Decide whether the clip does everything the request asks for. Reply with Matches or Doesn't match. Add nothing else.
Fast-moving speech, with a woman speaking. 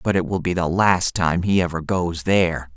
Doesn't match